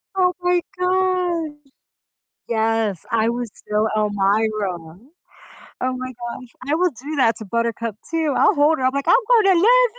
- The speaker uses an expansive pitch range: Yes, wide, 7.6 semitones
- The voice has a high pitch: Yes, very high, 255 Hz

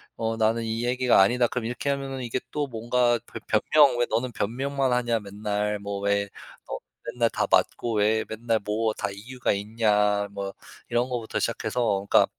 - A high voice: No, low, 115 Hz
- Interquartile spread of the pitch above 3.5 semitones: No, average, 3.0 semitones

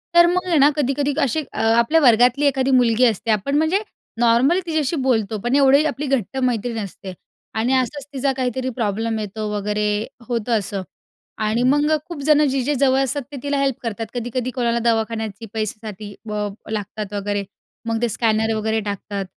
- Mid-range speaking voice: No, high, 240 Hz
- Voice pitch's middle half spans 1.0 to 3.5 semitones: No, average, 4.0 semitones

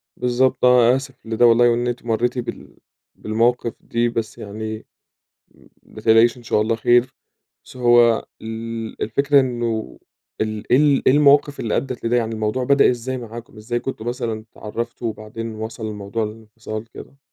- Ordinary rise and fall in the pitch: No, narrow, 1.9 semitones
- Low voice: Yes, low, 115 Hz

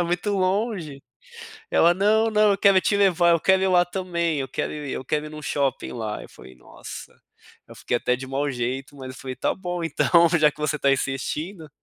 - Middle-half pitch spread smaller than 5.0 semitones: No, wide, 5.5 semitones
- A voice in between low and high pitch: Yes, medium, 160 Hz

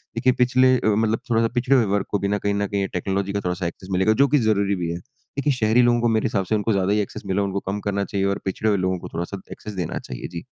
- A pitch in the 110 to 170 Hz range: No, low, 100 Hz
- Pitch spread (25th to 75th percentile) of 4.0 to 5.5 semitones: No, average, 2.9 semitones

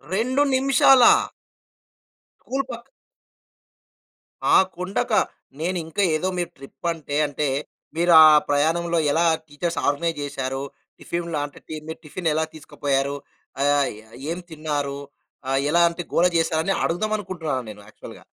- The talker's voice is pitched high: No, medium, 160 Hz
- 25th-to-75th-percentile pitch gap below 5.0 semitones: Yes, average, 3.5 semitones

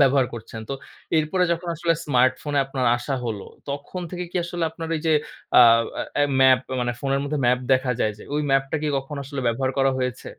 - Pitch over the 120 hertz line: Yes, low, 135 Hz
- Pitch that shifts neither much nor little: Yes, average, 3.1 semitones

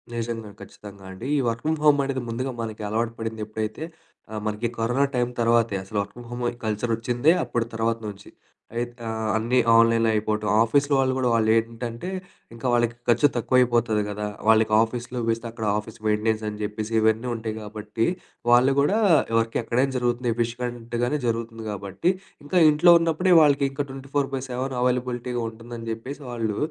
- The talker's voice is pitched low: Yes, low, 115 Hz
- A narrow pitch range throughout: Yes, narrow, 2.2 semitones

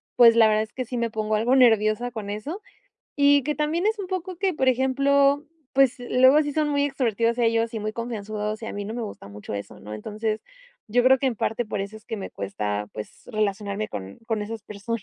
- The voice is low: No, high, 230 Hz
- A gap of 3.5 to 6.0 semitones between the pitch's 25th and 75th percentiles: Yes, average, 4.0 semitones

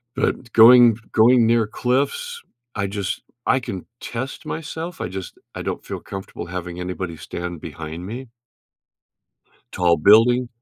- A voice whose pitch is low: Yes, low, 110 Hz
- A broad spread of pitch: Yes, wide, 5.7 semitones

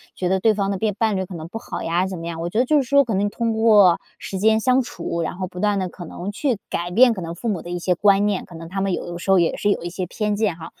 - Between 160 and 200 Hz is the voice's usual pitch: Yes, high, 195 Hz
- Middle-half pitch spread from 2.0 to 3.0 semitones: No, average, 3.7 semitones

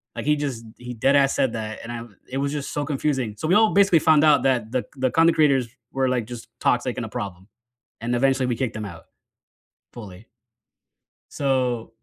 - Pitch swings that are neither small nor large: Yes, average, 3.6 semitones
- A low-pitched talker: Yes, low, 130 Hz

